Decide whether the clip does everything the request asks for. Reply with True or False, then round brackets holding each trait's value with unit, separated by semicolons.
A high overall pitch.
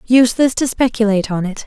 True (230 Hz)